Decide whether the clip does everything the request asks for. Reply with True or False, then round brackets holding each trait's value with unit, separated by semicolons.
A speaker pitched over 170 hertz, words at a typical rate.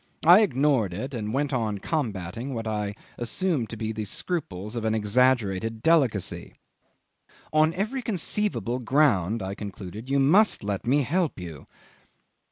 False (120 Hz; 145 wpm)